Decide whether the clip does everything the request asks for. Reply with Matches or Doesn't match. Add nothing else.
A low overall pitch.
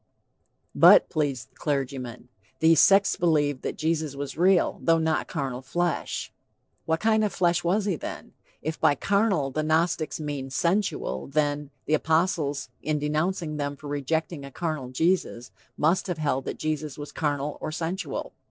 Doesn't match